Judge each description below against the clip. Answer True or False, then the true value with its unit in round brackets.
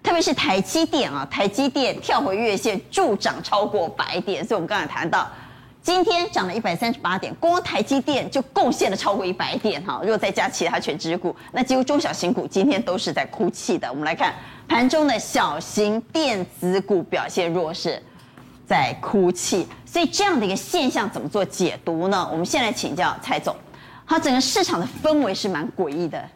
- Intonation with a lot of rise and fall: True (8.2 semitones)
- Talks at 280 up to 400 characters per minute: True (300 characters per minute)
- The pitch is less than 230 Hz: False (260 Hz)